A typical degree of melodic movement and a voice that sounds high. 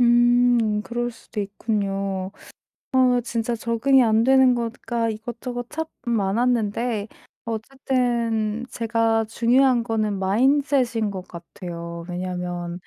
Yes: average, 3.0 semitones; high, 230 Hz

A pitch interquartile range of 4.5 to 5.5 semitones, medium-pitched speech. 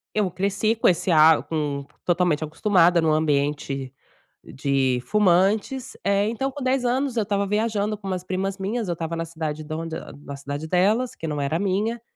Yes: average, 5.2 semitones; medium, 180 Hz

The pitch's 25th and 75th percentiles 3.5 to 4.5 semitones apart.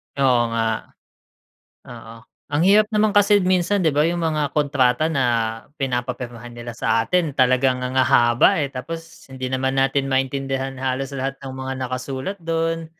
Yes: average, 4.2 semitones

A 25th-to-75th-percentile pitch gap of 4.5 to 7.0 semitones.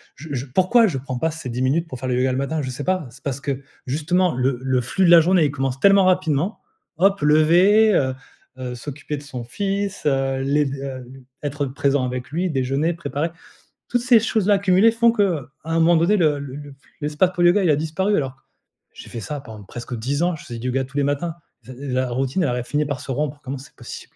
Yes: average, 5.0 semitones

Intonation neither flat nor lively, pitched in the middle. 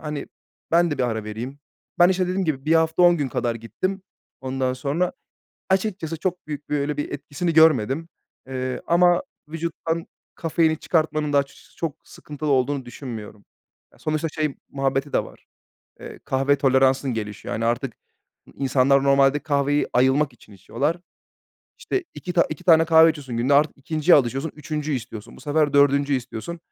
Yes: average, 3.5 semitones; medium, 145 Hz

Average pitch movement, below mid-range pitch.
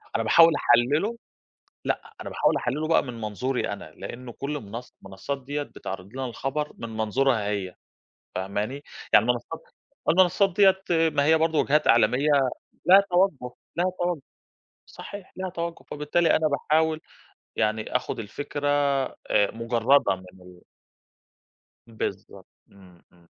No: wide, 6.7 semitones; low, 130 Hz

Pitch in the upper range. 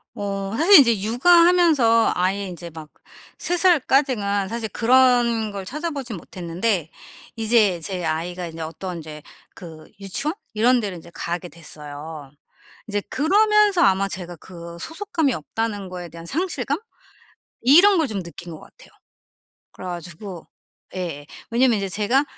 Yes: high, 205 Hz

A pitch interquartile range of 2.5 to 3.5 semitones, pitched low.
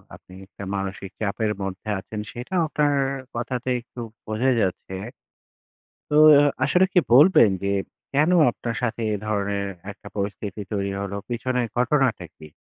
No: average, 4.2 semitones; low, 110 Hz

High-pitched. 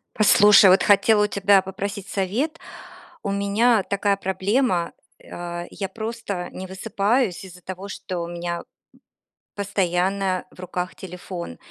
Yes: high, 195 Hz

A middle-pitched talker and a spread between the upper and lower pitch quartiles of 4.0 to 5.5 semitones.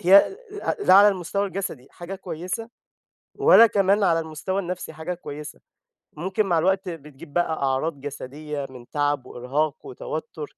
Yes: medium, 165 Hz; average, 4.6 semitones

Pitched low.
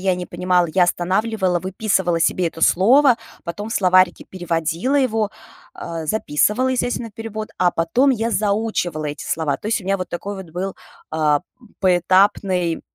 No: medium, 185 Hz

